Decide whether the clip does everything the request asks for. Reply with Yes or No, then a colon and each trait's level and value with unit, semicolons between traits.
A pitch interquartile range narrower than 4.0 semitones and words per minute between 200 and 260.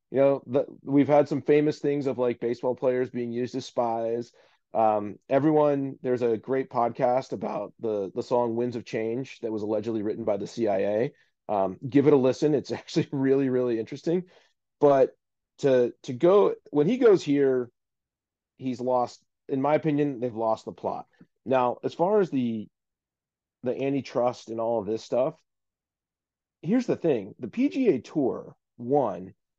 No: average, 3.4 semitones; average, 165 wpm